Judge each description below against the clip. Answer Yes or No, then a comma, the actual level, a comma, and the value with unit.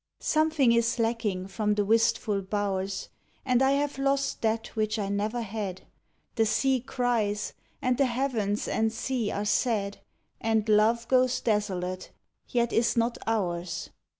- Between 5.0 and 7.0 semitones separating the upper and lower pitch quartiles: No, average, 3.0 semitones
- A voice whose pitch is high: Yes, high, 225 Hz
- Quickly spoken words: No, average, 150 wpm